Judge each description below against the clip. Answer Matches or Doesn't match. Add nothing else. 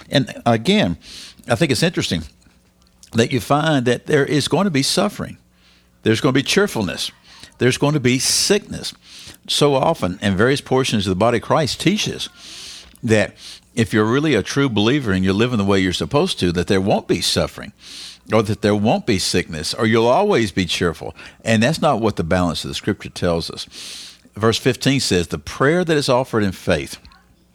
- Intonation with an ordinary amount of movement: Doesn't match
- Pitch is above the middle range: Doesn't match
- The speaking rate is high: Doesn't match